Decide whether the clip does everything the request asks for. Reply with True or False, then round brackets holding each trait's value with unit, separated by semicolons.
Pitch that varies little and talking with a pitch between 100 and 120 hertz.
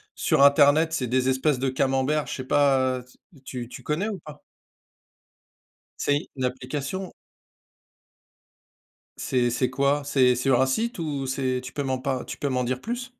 False (2.3 semitones; 135 Hz)